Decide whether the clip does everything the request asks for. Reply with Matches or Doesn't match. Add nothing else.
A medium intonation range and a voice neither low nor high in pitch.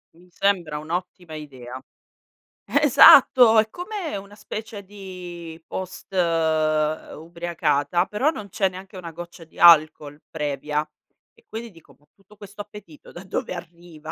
Matches